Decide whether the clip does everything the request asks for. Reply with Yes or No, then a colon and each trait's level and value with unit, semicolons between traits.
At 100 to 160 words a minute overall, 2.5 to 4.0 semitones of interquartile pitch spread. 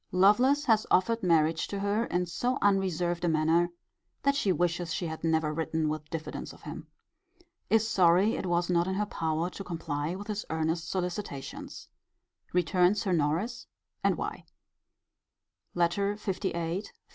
Yes: average, 150 wpm; average, 3.6 semitones